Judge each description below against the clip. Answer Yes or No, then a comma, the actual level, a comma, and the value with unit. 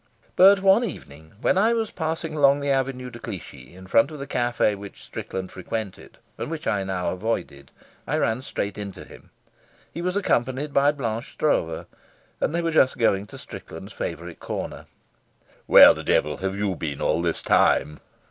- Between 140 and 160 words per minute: No, average, 175 wpm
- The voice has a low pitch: Yes, low, 120 Hz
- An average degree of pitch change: No, wide, 8.1 semitones